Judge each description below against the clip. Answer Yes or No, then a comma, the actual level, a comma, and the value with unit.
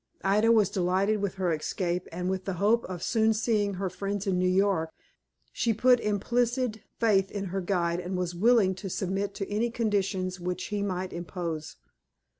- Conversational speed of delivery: Yes, average, 180 wpm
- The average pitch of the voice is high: Yes, high, 195 Hz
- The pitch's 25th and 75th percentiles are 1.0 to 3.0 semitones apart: Yes, average, 2.7 semitones